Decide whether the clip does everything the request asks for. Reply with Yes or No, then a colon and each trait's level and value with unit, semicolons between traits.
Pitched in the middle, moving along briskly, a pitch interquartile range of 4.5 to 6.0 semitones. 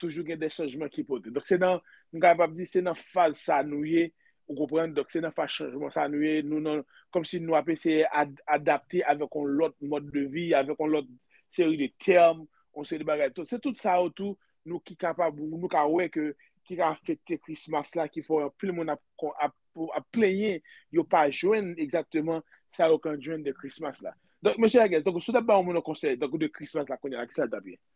No: medium, 165 Hz; fast, 230 wpm; average, 3.0 semitones